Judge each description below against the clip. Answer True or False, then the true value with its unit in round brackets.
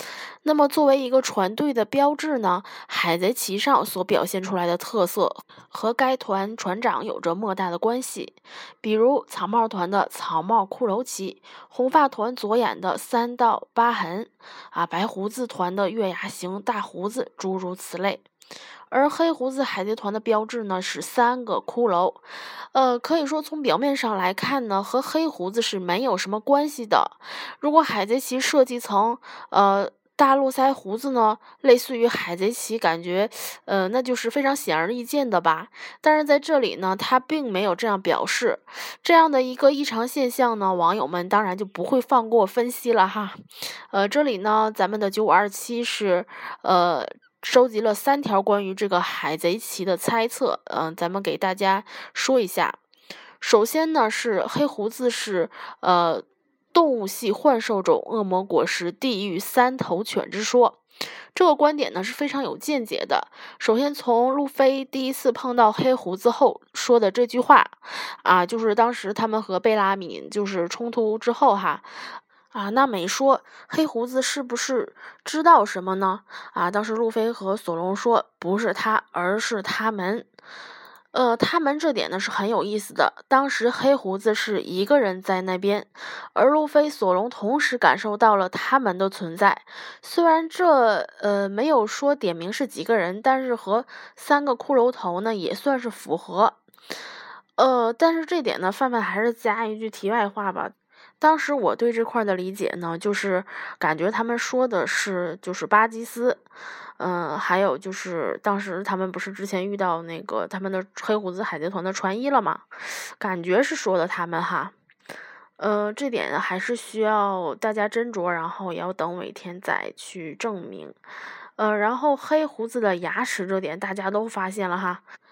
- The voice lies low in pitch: False (220 Hz)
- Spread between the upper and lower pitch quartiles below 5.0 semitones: False (5.3 semitones)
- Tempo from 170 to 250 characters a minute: True (245 characters per minute)